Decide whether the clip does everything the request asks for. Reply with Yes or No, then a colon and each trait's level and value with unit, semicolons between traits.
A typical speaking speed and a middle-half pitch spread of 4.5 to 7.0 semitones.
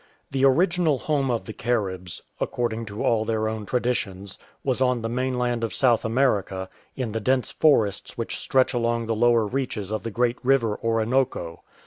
No: average, 175 wpm; average, 2.8 semitones